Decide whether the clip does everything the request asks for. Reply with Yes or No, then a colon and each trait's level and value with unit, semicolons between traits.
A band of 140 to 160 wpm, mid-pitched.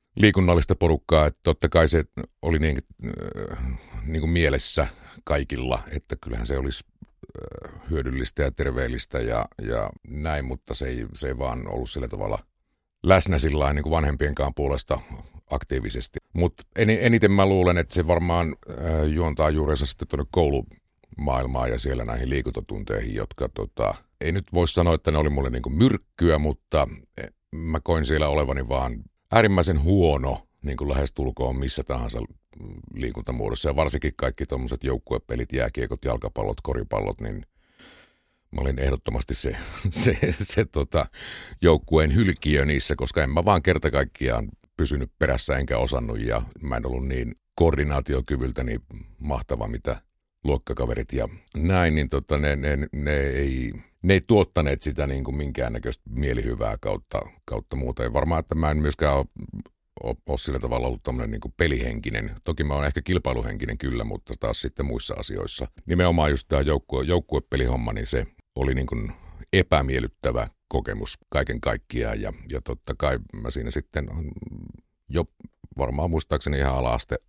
No: average, 145 wpm; very low, 75 Hz